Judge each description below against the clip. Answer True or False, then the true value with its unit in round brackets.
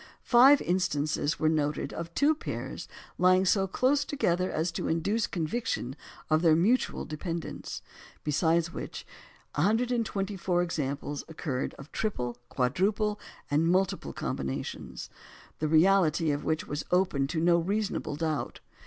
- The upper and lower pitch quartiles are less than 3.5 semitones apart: False (4.2 semitones)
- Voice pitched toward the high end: False (170 Hz)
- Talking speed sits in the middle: False (130 wpm)